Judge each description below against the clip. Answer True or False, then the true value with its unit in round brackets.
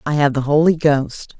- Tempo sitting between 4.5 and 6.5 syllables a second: True (4.8 syllables/s)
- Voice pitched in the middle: True (145 Hz)